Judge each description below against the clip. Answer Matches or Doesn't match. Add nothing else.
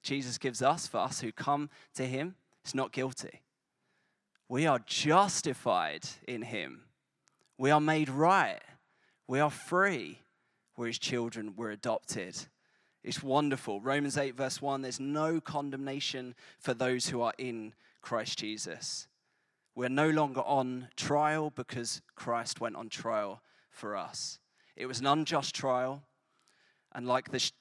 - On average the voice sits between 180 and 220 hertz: Doesn't match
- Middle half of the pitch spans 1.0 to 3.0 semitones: Matches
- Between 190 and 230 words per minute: Doesn't match